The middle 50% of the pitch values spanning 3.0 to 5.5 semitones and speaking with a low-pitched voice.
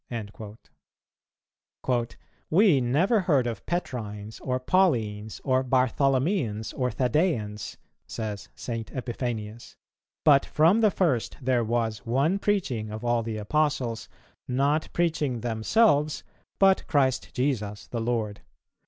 Yes: average, 5.1 semitones; low, 125 Hz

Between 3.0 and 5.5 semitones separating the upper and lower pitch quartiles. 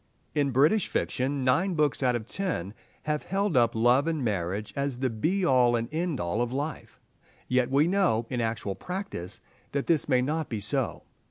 Yes: average, 5.2 semitones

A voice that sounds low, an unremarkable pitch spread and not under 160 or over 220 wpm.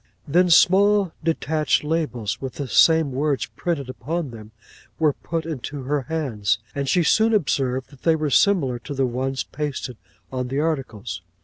No: medium, 145 Hz; average, 4.0 semitones; average, 165 wpm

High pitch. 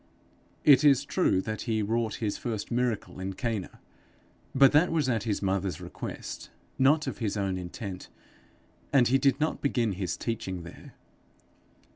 No: low, 115 Hz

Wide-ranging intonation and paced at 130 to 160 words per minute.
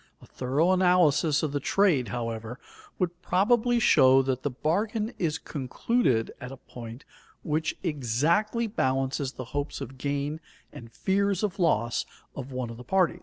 Yes: wide, 6.2 semitones; average, 155 wpm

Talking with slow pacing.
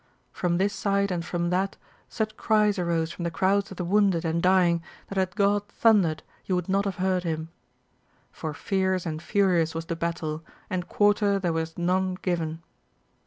No: average, 180 wpm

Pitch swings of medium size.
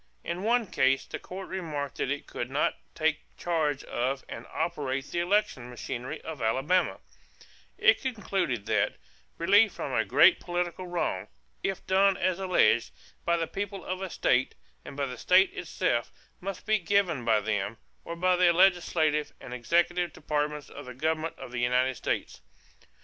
No: wide, 5.8 semitones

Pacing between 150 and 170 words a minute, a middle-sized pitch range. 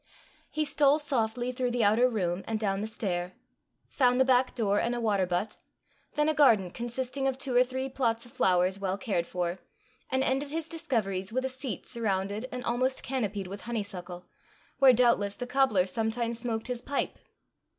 No: average, 180 wpm; average, 4.5 semitones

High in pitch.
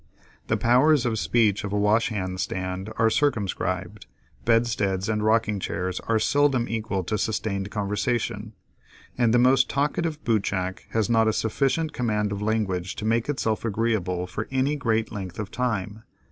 No: low, 110 Hz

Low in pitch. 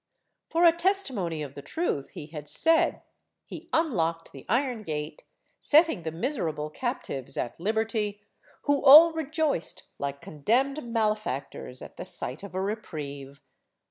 No: high, 210 Hz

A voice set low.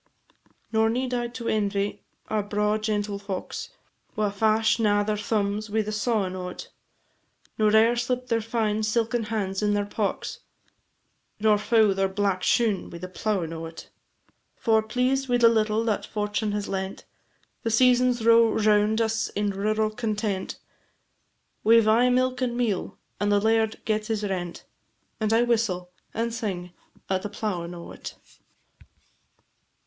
No: high, 215 Hz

